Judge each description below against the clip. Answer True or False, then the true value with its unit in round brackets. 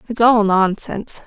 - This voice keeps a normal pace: True (145 wpm)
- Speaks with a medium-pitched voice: False (210 Hz)